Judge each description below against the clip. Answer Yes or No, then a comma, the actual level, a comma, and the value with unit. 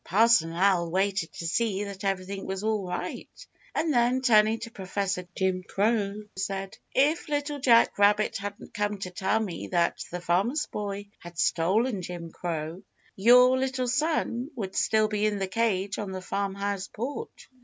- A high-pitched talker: Yes, high, 200 Hz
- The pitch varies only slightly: No, average, 3.7 semitones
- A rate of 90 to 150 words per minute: No, average, 165 wpm